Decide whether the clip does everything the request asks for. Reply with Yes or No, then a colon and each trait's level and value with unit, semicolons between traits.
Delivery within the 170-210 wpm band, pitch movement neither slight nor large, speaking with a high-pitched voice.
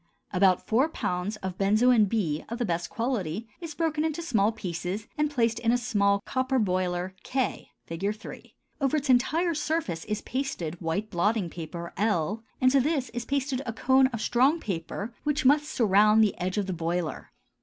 No: average, 180 wpm; wide, 6.1 semitones; high, 220 Hz